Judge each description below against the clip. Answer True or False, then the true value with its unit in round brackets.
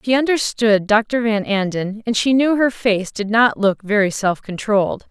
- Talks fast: False (190 wpm)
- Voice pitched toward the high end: True (220 Hz)